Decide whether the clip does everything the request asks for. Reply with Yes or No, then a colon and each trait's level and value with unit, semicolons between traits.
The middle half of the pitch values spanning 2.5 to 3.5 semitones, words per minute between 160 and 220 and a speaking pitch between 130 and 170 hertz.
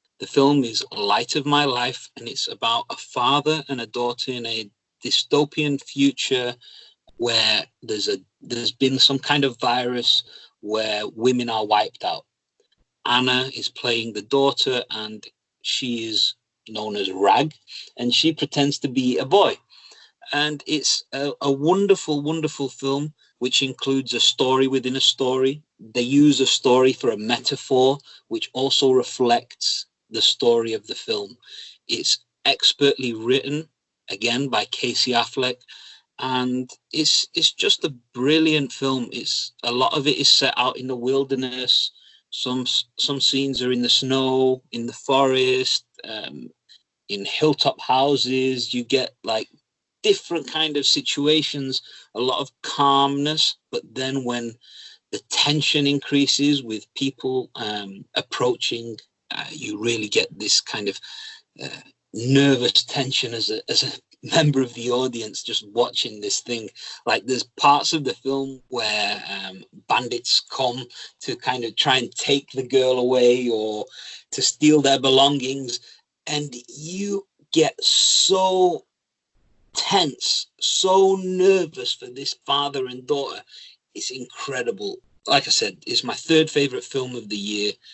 No: average, 2.9 semitones; average, 145 wpm; low, 135 Hz